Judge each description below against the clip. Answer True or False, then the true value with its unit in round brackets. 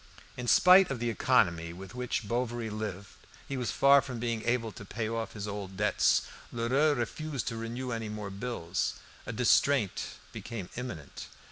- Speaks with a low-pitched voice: True (115 Hz)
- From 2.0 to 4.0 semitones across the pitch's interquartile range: True (3.2 semitones)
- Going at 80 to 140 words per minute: False (165 wpm)